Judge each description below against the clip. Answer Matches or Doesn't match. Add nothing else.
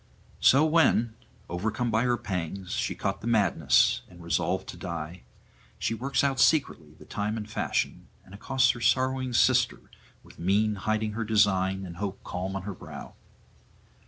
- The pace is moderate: Matches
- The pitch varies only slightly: Doesn't match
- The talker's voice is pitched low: Matches